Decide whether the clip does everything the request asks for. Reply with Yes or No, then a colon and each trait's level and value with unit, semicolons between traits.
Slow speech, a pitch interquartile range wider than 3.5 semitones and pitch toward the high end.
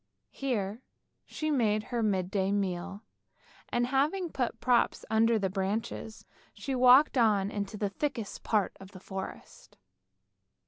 Yes: slow, 130 wpm; average, 4.2 semitones; high, 215 Hz